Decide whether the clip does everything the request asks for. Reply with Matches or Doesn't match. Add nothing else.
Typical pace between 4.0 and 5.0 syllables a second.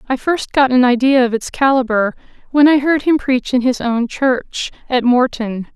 Matches